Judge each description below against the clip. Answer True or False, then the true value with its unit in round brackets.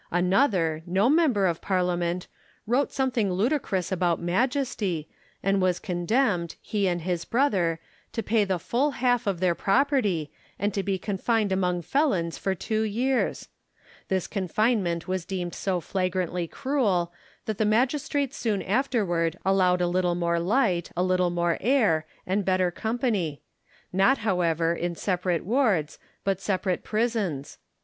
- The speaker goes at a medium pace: True (145 wpm)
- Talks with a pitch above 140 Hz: True (190 Hz)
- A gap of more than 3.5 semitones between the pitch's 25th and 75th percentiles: True (4.4 semitones)